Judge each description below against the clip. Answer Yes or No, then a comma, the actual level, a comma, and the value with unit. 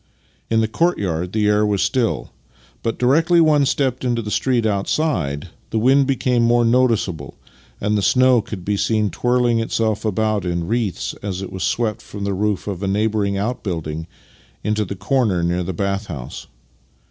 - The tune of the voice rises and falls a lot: No, average, 3.8 semitones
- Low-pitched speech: Yes, low, 105 Hz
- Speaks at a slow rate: No, average, 170 wpm